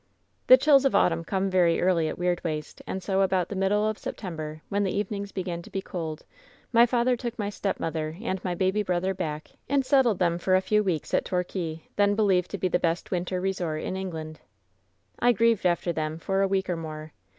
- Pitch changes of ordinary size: Yes, average, 3.3 semitones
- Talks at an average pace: No, fast, 215 wpm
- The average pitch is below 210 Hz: Yes, medium, 185 Hz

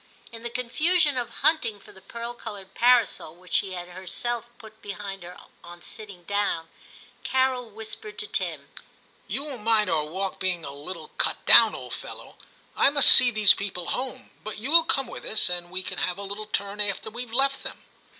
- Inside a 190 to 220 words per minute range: Yes, average, 200 wpm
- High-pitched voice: Yes, high, 215 Hz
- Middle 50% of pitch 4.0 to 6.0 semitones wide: Yes, average, 4.9 semitones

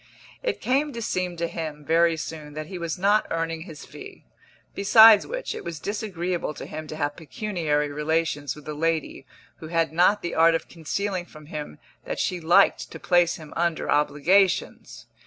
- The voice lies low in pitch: No, medium, 165 Hz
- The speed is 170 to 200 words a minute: Yes, average, 180 wpm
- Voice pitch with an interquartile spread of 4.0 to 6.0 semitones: No, average, 3.1 semitones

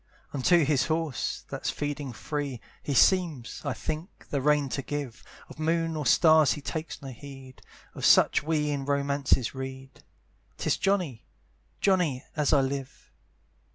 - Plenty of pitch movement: No, average, 2.9 semitones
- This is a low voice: No, medium, 145 Hz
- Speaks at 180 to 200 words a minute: No, average, 150 wpm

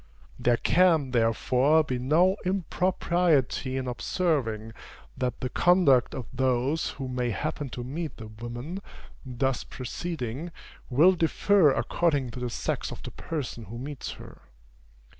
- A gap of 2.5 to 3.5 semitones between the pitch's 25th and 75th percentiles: No, average, 5.0 semitones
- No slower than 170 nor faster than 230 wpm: No, slow, 135 wpm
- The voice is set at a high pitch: No, low, 135 Hz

